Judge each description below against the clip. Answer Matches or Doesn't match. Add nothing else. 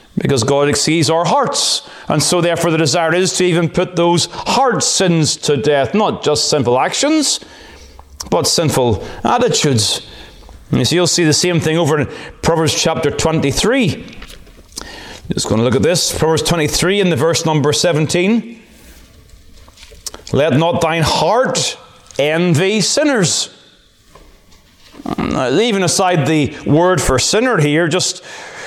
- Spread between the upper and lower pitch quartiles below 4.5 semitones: Matches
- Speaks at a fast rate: Doesn't match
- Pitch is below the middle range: Doesn't match